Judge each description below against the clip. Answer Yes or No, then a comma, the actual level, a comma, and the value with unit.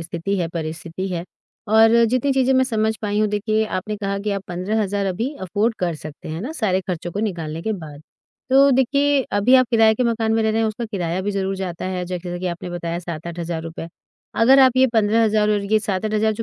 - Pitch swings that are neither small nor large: Yes, average, 4.1 semitones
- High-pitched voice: Yes, high, 205 Hz